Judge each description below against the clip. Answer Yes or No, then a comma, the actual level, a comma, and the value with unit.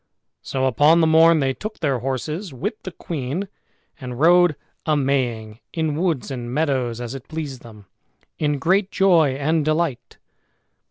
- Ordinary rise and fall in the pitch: Yes, average, 4.1 semitones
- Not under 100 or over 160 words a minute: Yes, average, 155 wpm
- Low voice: No, medium, 145 Hz